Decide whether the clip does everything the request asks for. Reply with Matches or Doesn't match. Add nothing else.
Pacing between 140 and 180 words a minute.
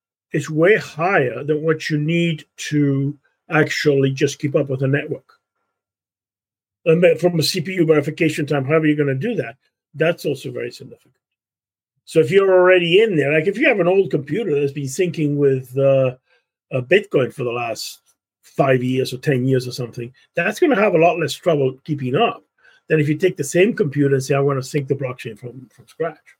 Doesn't match